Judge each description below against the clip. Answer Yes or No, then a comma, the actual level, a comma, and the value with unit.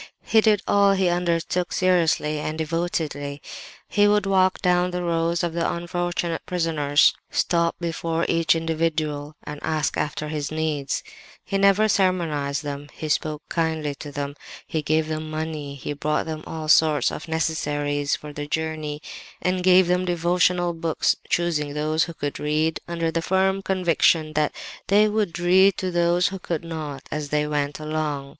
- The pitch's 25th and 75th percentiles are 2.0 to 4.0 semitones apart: Yes, average, 2.8 semitones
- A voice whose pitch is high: No, medium, 160 Hz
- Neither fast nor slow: Yes, average, 160 wpm